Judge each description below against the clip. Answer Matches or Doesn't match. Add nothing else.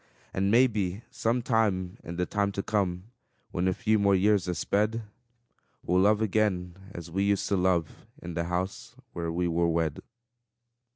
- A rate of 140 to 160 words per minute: Doesn't match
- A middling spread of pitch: Matches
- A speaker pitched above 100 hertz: Doesn't match